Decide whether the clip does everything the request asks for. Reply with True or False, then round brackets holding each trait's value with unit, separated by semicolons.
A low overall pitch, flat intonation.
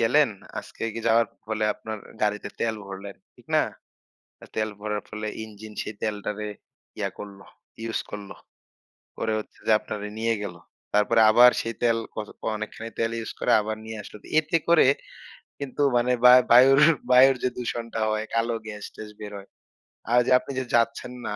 True (110 Hz; 2.0 semitones)